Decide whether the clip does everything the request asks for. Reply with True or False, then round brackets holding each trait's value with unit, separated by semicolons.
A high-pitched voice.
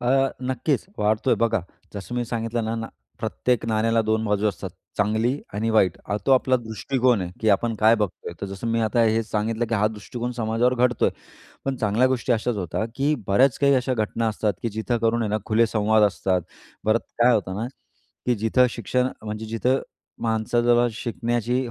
False (115 Hz)